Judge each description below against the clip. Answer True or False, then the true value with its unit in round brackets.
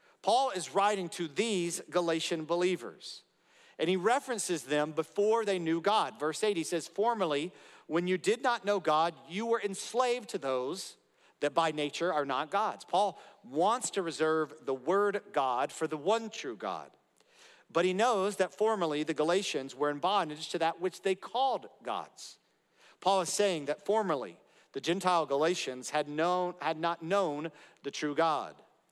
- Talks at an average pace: True (170 wpm)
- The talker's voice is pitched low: False (180 Hz)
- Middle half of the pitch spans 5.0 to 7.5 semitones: False (4.3 semitones)